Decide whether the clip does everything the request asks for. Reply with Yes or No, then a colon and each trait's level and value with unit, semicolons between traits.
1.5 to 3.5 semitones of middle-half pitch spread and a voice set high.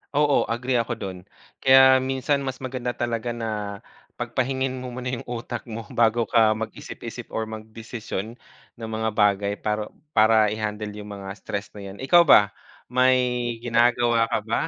No: average, 2.8 semitones; low, 115 Hz